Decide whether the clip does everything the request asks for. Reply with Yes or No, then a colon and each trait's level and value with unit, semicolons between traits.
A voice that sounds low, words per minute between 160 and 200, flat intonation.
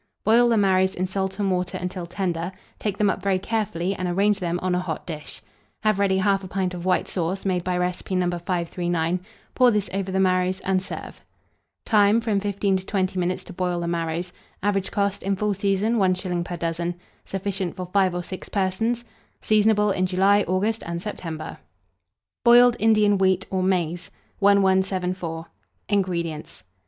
No: high, 190 Hz; average, 170 wpm; narrow, 2.0 semitones